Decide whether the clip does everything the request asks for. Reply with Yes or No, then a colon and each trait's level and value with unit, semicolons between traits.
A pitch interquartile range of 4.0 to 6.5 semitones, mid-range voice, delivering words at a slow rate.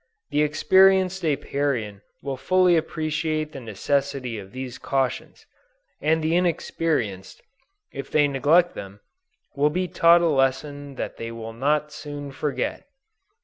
No: average, 3.4 semitones; medium, 145 Hz; slow, 130 wpm